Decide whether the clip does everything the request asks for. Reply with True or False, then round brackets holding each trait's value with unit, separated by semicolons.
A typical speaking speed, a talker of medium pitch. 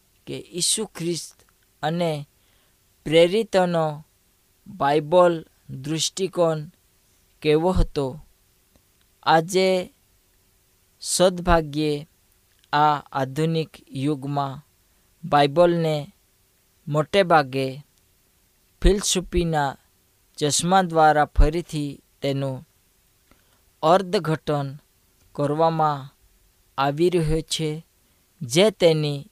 False (55 wpm; 150 Hz)